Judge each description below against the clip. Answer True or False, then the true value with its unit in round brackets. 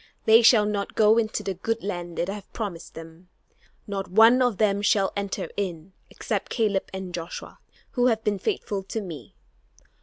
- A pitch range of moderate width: True (3.0 semitones)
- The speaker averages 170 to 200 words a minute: True (180 wpm)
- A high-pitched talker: True (200 Hz)